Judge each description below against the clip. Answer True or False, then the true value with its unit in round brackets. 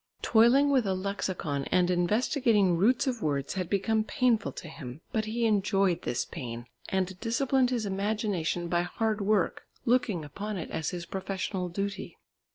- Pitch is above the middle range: True (195 Hz)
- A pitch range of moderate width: True (4.2 semitones)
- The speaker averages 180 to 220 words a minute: False (160 wpm)